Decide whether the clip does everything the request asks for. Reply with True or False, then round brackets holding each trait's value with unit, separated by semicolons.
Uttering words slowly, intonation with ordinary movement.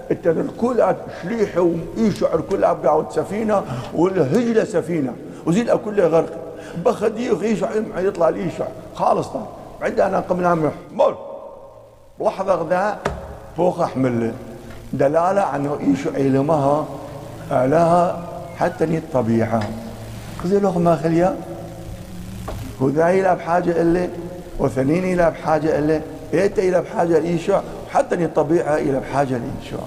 True (105 wpm; 4.2 semitones)